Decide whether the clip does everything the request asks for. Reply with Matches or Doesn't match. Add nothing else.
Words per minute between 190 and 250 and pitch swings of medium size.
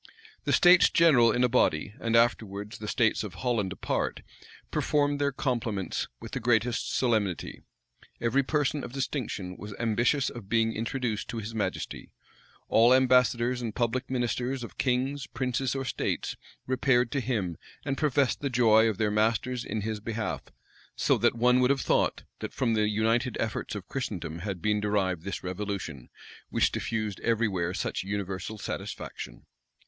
Doesn't match